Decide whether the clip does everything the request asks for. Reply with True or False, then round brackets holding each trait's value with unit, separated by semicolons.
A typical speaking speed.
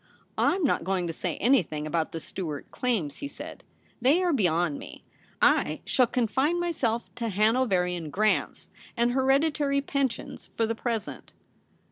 True (155 wpm)